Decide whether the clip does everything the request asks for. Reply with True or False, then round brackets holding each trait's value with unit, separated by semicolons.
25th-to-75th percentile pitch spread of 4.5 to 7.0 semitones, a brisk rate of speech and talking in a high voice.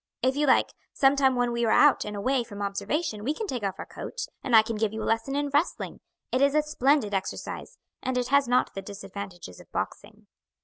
True (5.1 semitones; 225 wpm; 245 Hz)